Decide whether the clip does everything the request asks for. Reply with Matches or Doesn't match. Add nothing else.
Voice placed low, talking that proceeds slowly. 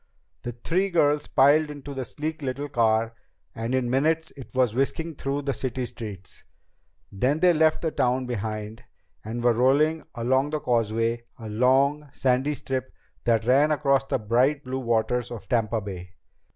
Doesn't match